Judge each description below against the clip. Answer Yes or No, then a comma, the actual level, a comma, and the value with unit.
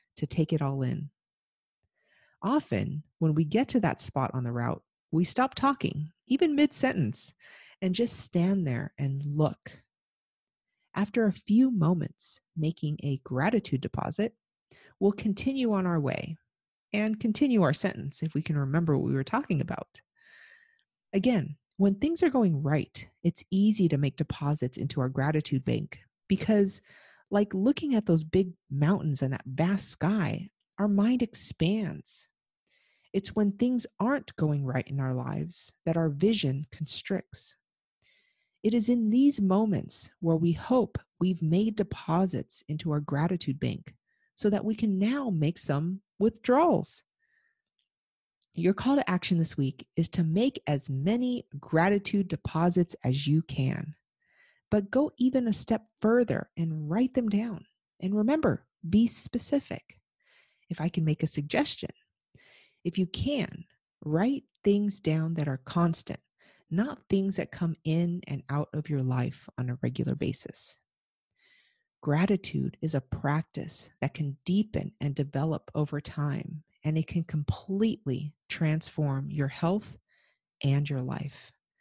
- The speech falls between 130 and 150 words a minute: Yes, average, 145 wpm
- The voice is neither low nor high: Yes, medium, 170 Hz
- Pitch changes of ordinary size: No, wide, 6.4 semitones